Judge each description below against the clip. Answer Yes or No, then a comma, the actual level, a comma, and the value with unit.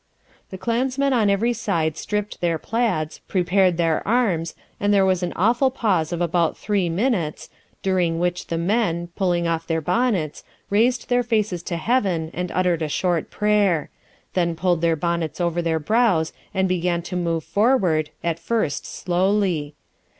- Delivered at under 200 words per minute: Yes, average, 160 wpm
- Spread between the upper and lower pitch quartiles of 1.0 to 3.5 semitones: No, average, 4.0 semitones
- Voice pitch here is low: No, medium, 180 Hz